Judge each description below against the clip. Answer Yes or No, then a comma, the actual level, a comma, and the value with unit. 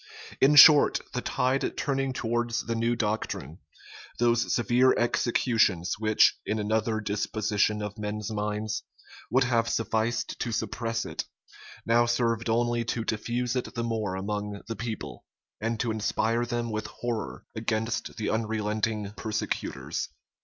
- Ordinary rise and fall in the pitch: No, narrow, 1.8 semitones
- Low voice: Yes, low, 115 Hz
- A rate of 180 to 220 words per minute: No, slow, 135 wpm